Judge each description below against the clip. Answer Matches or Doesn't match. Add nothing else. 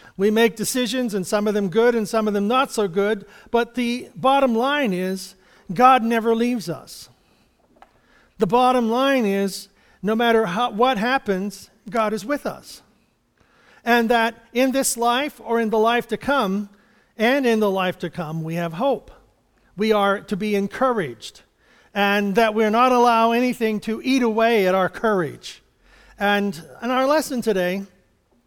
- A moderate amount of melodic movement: Matches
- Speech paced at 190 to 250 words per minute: Doesn't match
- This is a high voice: Matches